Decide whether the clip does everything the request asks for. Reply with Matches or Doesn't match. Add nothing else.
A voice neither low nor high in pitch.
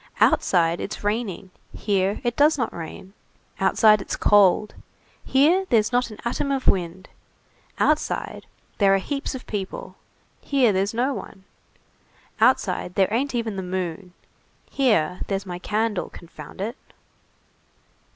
Doesn't match